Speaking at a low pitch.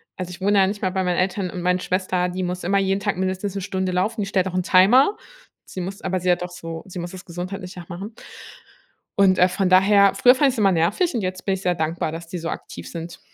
No: medium, 185 Hz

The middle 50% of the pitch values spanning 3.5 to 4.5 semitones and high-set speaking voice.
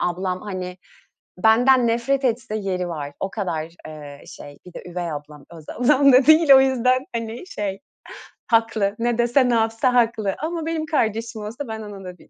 No: wide, 5.6 semitones; high, 225 Hz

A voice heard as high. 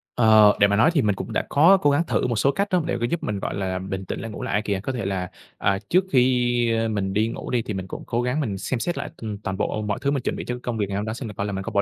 No: low, 110 Hz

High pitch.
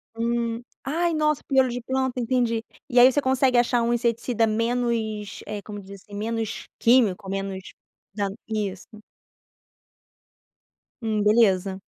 Yes: high, 230 Hz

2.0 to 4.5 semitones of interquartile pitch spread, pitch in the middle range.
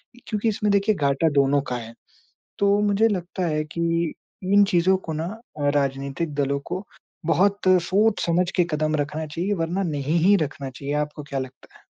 No: average, 5.3 semitones; medium, 165 Hz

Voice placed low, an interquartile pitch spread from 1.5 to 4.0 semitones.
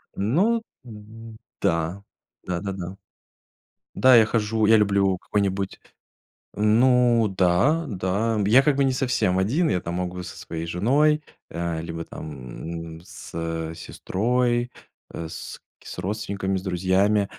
No: low, 100 Hz; average, 5.2 semitones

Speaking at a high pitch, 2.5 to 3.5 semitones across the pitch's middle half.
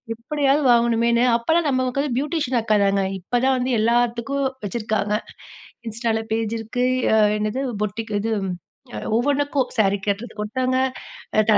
Yes: high, 235 Hz; average, 3.2 semitones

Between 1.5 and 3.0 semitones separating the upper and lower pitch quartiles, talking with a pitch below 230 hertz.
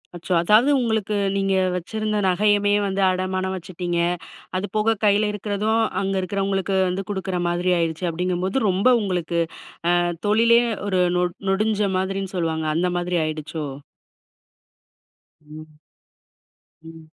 Yes: average, 2.7 semitones; high, 190 Hz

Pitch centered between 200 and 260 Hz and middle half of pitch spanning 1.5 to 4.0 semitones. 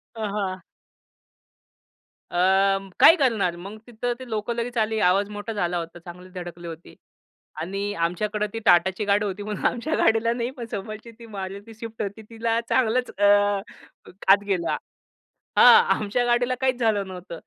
Yes: high, 210 Hz; average, 3.5 semitones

